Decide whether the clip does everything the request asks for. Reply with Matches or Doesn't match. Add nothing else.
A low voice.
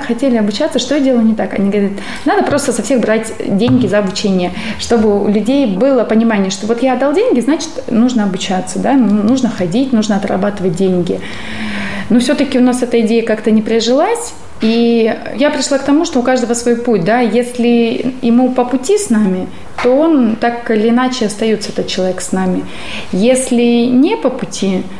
Doesn't match